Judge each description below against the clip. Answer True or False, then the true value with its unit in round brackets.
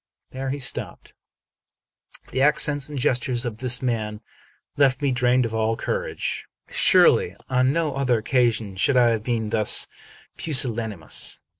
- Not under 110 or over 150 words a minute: True (140 wpm)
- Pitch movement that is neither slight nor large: True (3.0 semitones)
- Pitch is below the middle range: True (125 Hz)